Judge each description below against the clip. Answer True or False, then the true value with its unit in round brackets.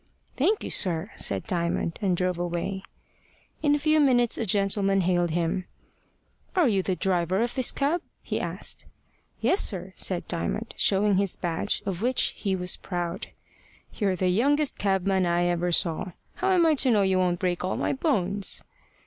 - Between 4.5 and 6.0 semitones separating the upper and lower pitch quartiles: True (4.9 semitones)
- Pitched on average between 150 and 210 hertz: True (190 Hz)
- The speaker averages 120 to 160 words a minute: False (175 wpm)